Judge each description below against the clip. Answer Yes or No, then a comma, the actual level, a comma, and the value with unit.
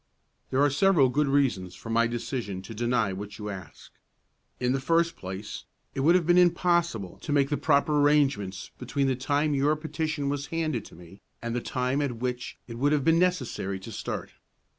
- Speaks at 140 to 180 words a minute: No, average, 195 wpm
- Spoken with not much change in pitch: No, average, 4.6 semitones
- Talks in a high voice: No, low, 135 Hz